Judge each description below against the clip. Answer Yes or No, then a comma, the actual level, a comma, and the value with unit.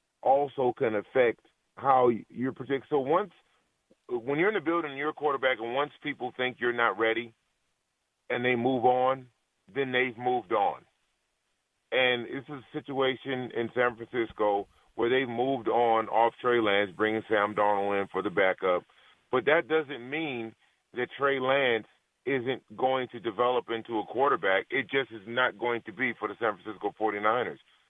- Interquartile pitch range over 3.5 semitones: No, average, 2.7 semitones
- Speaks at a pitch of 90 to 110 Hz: No, low, 125 Hz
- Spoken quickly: No, average, 170 wpm